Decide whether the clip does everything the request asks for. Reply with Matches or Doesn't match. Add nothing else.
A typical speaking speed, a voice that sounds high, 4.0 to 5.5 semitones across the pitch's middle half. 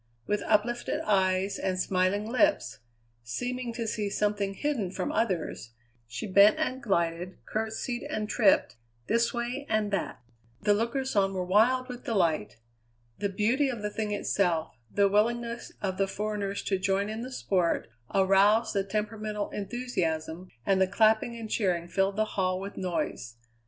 Doesn't match